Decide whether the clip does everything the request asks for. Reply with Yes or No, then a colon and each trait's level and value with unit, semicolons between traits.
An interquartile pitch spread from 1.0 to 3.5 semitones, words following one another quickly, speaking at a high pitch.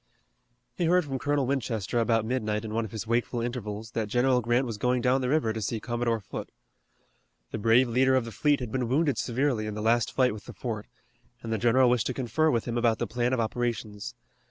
No: narrow, 2.5 semitones; fast, 230 wpm; low, 120 Hz